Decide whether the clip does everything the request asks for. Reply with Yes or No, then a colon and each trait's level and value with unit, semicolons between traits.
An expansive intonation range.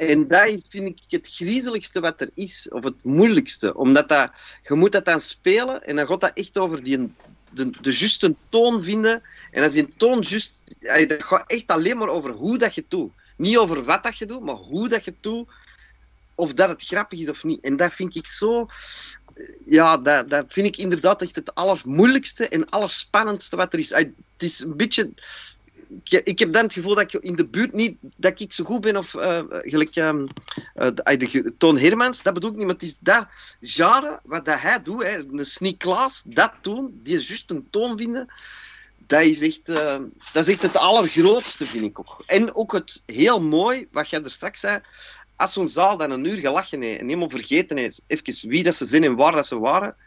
Yes: wide, 5.9 semitones